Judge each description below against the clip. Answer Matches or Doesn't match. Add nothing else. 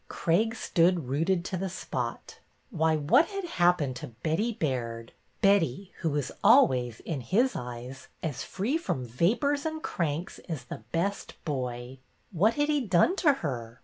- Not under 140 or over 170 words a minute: Matches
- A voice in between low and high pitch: Matches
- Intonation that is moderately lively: Doesn't match